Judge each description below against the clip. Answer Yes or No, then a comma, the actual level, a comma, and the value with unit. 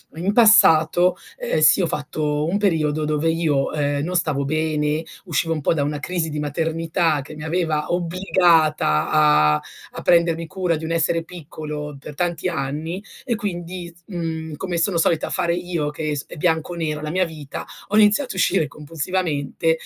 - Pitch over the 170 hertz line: No, medium, 160 Hz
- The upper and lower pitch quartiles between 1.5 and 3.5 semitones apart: Yes, narrow, 2.5 semitones